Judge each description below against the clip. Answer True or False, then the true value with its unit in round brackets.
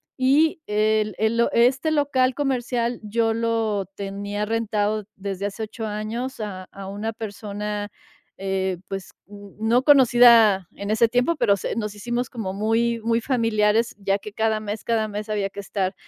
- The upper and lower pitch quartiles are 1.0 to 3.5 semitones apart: True (2.5 semitones)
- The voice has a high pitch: True (215 Hz)